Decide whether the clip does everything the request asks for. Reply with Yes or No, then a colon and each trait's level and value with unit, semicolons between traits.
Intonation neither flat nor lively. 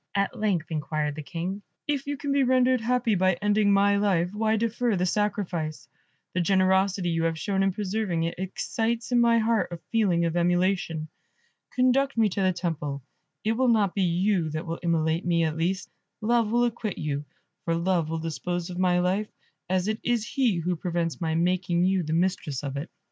Yes: average, 4.4 semitones